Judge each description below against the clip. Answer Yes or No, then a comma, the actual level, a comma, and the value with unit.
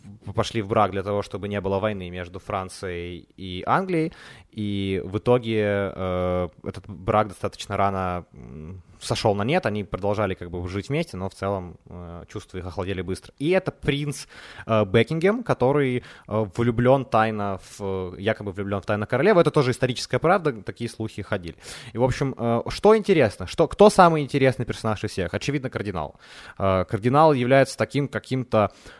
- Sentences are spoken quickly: Yes, fast, 165 wpm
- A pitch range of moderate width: Yes, average, 4.7 semitones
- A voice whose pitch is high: No, low, 105 Hz